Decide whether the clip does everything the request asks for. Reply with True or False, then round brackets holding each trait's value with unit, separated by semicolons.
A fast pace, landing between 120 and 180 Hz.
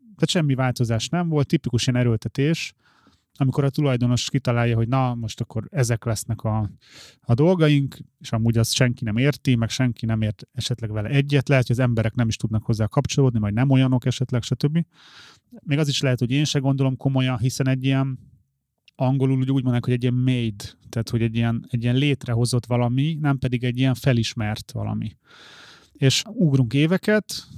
True (185 wpm; 130 Hz)